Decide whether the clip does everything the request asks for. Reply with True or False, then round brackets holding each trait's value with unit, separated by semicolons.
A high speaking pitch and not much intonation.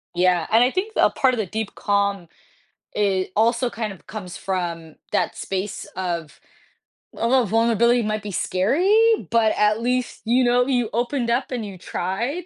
False (220 Hz; 4.4 semitones)